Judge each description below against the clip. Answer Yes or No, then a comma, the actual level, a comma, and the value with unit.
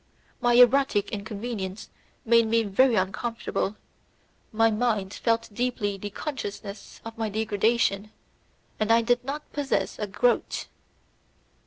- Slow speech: Yes, slow, 120 wpm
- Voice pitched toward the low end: No, high, 225 Hz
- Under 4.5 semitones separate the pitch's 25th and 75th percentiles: Yes, average, 2.9 semitones